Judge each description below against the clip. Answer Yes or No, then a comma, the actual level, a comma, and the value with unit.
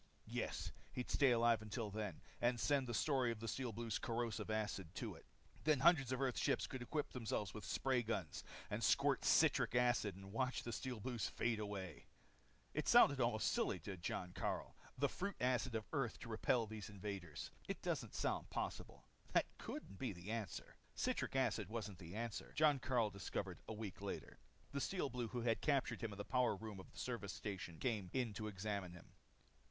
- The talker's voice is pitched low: Yes, low, 115 Hz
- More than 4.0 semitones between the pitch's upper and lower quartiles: No, average, 3.6 semitones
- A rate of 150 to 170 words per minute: No, average, 195 wpm